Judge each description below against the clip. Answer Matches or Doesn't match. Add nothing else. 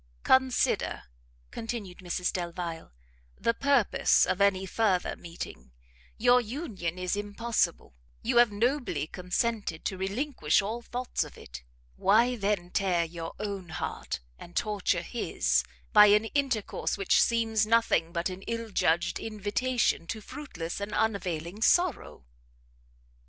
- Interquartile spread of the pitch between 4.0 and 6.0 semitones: Matches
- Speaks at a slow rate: Matches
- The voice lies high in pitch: Matches